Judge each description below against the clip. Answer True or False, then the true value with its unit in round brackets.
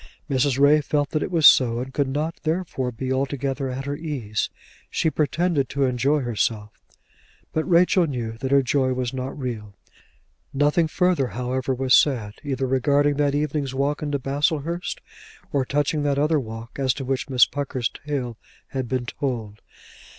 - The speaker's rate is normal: True (165 wpm)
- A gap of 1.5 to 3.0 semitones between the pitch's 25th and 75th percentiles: True (2.5 semitones)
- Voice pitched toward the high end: False (135 Hz)